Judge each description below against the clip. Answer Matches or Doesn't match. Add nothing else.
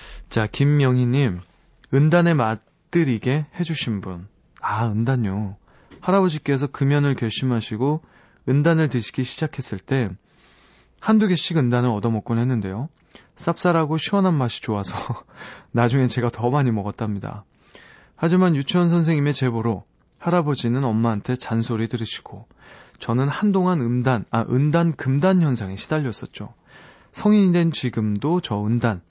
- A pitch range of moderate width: Doesn't match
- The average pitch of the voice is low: Matches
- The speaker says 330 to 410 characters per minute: Doesn't match